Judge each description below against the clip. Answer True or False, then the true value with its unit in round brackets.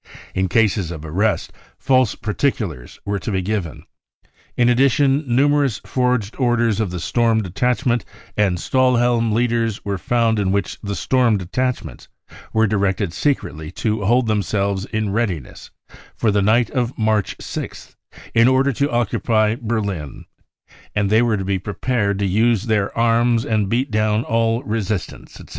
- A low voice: True (110 Hz)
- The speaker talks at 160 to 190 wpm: False (150 wpm)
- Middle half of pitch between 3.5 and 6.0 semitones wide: False (3.1 semitones)